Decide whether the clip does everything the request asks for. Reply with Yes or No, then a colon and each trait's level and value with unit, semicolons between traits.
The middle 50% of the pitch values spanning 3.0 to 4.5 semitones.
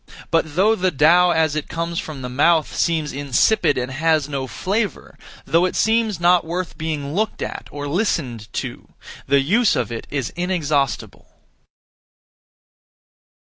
Yes: average, 4.1 semitones